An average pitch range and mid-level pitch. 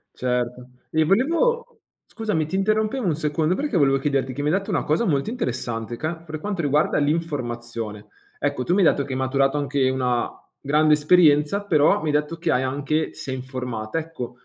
Yes: average, 4.5 semitones; medium, 150 Hz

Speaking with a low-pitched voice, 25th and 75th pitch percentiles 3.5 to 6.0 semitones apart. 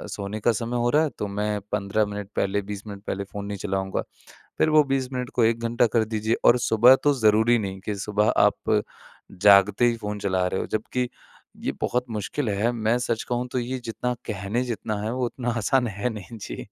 No: low, 110 Hz; average, 3.0 semitones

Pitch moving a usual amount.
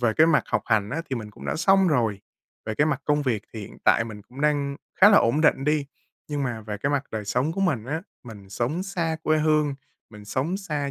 No: wide, 5.7 semitones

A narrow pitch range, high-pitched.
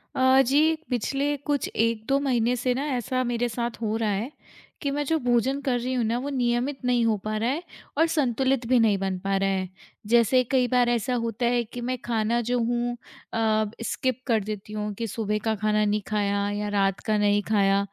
No: average, 3.2 semitones; high, 235 Hz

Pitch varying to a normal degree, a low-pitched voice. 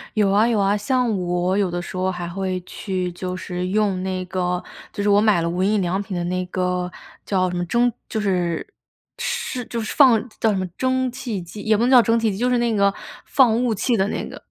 No: average, 3.8 semitones; high, 195 Hz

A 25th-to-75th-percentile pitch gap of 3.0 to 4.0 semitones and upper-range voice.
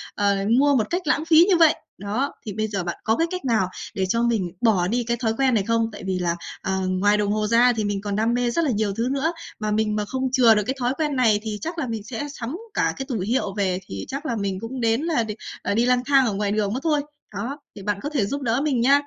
No: average, 4.4 semitones; high, 230 Hz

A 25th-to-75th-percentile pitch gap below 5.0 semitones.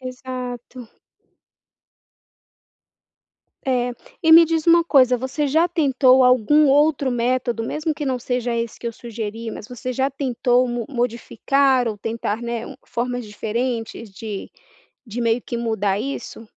Yes: narrow, 2.6 semitones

